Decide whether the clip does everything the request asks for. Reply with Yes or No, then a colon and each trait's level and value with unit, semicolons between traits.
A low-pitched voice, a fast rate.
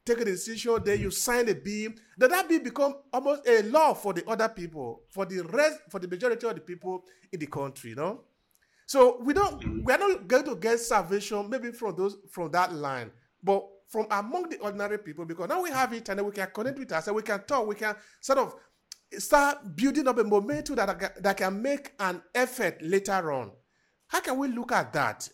No: high, 215 Hz; fast, 225 wpm